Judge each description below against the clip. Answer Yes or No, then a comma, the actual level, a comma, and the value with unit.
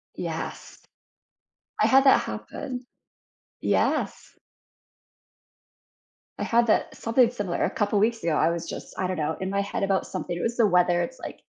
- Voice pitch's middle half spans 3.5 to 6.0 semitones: Yes, average, 4.9 semitones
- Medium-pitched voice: No, high, 200 Hz